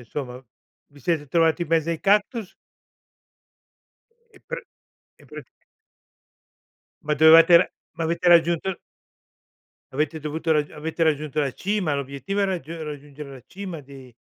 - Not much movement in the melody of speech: No, average, 3.0 semitones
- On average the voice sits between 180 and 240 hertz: No, medium, 160 Hz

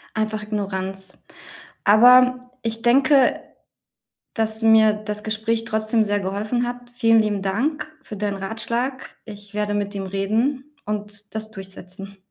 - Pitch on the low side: No, high, 215 Hz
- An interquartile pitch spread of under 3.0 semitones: Yes, narrow, 2.6 semitones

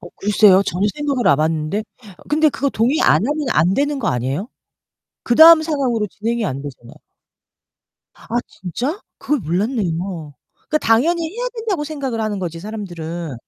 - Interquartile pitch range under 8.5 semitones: No, wide, 8.9 semitones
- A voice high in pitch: Yes, high, 220 Hz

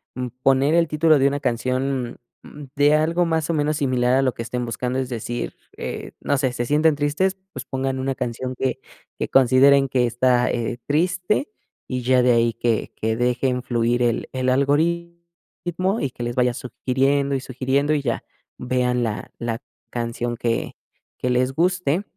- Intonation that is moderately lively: Yes, average, 3.1 semitones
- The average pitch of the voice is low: Yes, low, 130 Hz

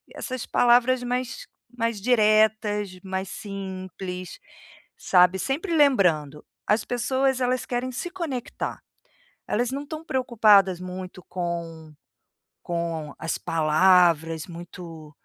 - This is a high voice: Yes, high, 195 Hz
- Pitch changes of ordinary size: No, wide, 6.1 semitones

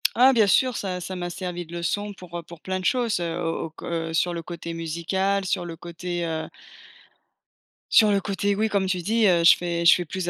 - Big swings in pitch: No, average, 2.8 semitones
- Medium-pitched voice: Yes, medium, 180 Hz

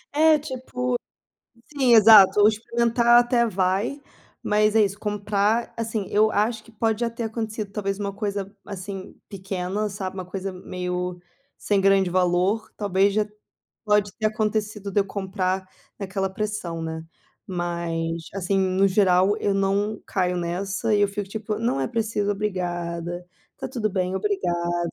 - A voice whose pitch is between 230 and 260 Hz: No, high, 200 Hz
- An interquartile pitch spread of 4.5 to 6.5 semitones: No, narrow, 2.6 semitones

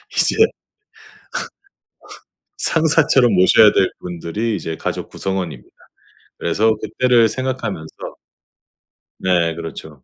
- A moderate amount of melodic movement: No, wide, 6.0 semitones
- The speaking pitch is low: Yes, low, 100 Hz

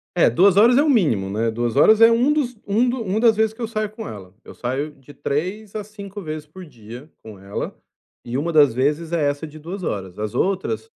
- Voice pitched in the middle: Yes, medium, 165 Hz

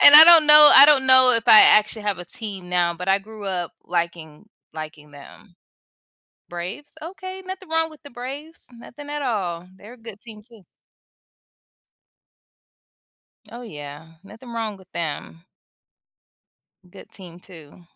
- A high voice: Yes, high, 210 Hz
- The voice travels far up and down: Yes, wide, 7.3 semitones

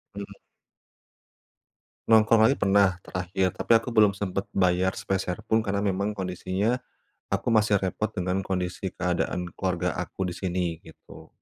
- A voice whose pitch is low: Yes, very low, 95 Hz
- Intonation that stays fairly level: Yes, narrow, 2.2 semitones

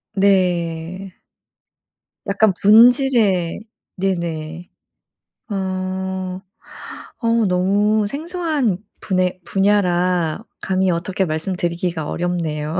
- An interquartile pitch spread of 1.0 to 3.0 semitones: Yes, average, 2.7 semitones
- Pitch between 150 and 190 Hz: Yes, medium, 185 Hz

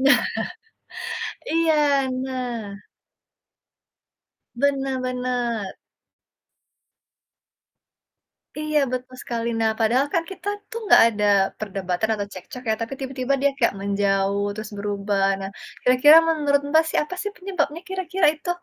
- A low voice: No, very high, 255 Hz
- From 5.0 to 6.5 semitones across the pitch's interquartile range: Yes, wide, 5.5 semitones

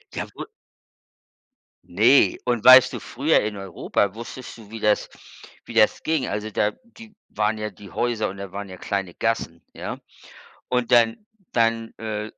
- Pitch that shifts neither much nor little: Yes, average, 3.0 semitones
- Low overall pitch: Yes, low, 110 Hz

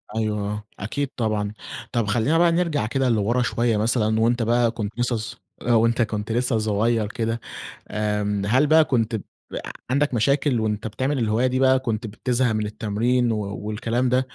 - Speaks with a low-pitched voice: Yes, low, 115 Hz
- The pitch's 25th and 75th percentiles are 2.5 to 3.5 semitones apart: Yes, average, 2.8 semitones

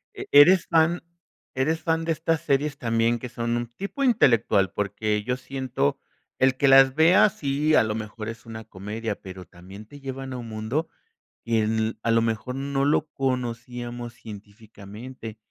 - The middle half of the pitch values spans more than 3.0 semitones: Yes, average, 4.0 semitones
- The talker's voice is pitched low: Yes, low, 120 Hz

